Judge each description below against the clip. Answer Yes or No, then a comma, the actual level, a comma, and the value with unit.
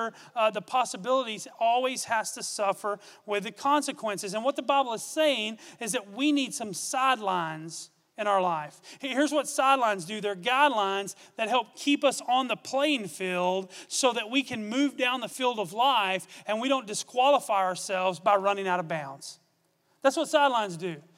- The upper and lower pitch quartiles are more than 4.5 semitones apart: Yes, wide, 5.6 semitones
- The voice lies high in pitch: Yes, high, 220 Hz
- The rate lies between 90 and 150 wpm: No, average, 180 wpm